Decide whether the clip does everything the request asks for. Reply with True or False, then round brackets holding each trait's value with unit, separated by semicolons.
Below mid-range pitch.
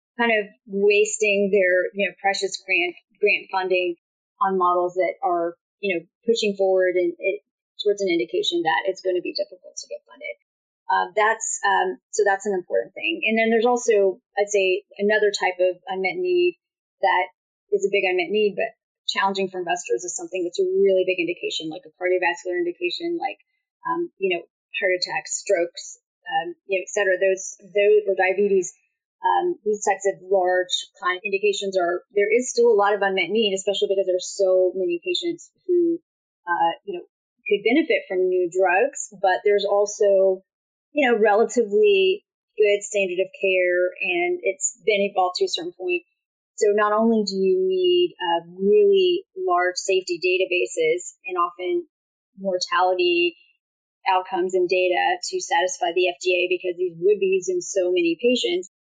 False (205 Hz)